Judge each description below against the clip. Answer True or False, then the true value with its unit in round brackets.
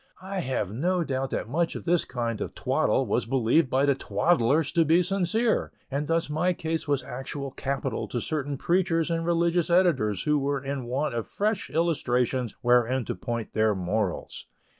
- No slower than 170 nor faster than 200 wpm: True (180 wpm)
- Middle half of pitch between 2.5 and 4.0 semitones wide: False (5.3 semitones)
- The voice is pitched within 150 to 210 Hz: False (140 Hz)